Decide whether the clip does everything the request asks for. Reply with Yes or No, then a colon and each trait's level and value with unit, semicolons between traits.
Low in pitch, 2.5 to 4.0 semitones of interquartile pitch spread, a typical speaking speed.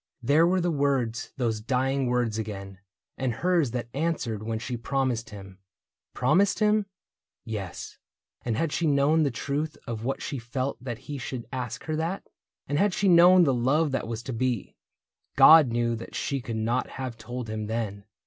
No: low, 125 Hz; average, 4.4 semitones; average, 180 wpm